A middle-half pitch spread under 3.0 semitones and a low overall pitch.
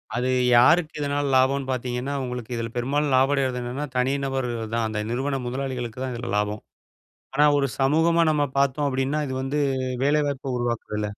Yes: narrow, 2.6 semitones; low, 130 Hz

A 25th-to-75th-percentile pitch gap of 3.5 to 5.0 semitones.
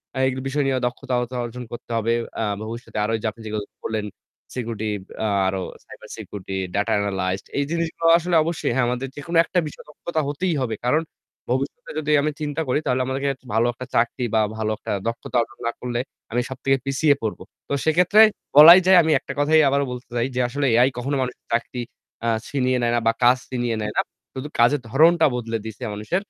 Yes: average, 4.1 semitones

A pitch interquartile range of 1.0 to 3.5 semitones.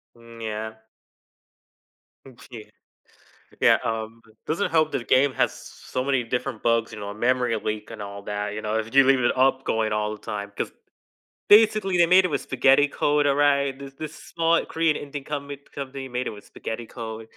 No: average, 4.4 semitones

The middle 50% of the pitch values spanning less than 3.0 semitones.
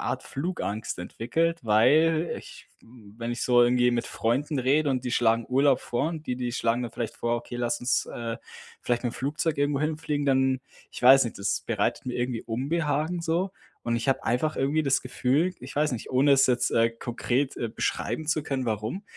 No: average, 3.9 semitones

